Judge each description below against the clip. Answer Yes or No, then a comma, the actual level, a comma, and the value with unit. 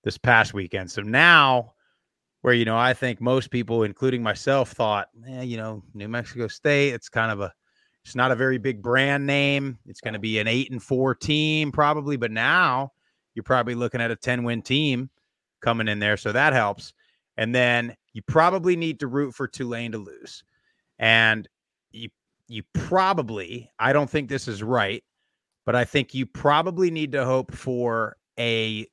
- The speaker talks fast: No, average, 185 wpm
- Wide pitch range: No, average, 3.4 semitones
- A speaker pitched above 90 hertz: Yes, low, 125 Hz